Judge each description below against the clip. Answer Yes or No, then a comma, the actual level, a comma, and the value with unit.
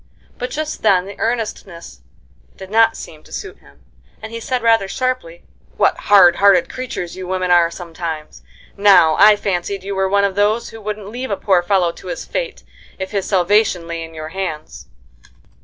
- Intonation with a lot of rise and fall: No, average, 3.6 semitones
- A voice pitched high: Yes, high, 195 Hz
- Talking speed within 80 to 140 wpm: No, average, 185 wpm